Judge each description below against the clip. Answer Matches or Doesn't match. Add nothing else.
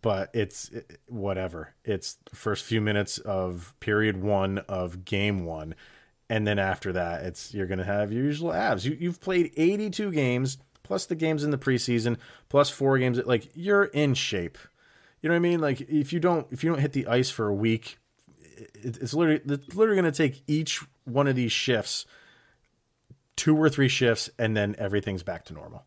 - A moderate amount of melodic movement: Doesn't match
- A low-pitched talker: Matches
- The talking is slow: Doesn't match